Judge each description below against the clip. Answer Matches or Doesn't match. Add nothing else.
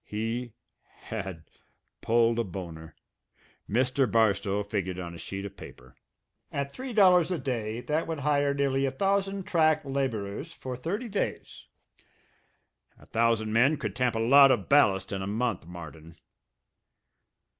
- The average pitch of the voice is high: Doesn't match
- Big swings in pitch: Matches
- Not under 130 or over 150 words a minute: Matches